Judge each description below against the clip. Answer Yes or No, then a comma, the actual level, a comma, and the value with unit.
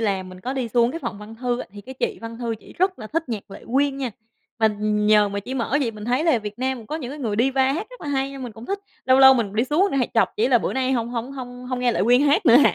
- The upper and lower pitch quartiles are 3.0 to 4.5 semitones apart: Yes, average, 3.3 semitones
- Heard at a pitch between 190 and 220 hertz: No, high, 245 Hz